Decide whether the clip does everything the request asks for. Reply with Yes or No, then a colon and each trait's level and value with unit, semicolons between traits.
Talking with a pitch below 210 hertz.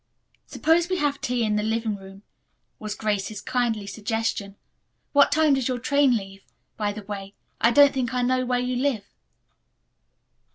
No: high, 235 Hz